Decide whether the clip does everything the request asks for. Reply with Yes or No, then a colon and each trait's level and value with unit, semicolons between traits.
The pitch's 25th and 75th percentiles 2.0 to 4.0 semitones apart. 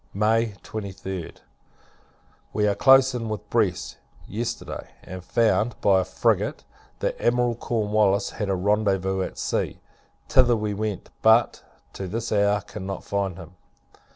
Yes: average, 2.7 semitones